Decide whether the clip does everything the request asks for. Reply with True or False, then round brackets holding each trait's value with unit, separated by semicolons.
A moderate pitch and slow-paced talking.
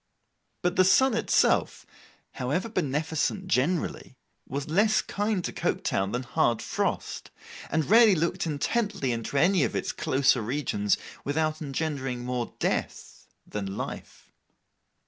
True (150 Hz; 125 wpm)